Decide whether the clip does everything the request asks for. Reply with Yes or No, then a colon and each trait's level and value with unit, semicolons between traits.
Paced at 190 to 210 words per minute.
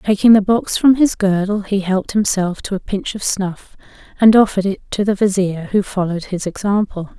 Yes: average, 200 wpm